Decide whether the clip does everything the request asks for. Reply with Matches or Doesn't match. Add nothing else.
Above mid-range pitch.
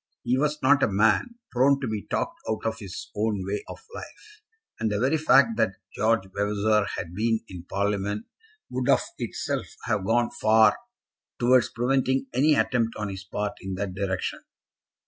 Doesn't match